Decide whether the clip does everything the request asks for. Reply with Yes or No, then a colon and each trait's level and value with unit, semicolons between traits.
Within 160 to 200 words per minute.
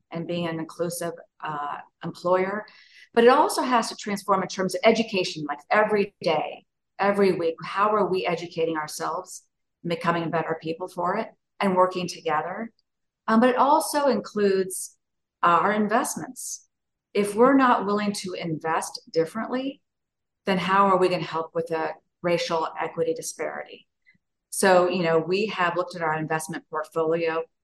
No: average, 150 wpm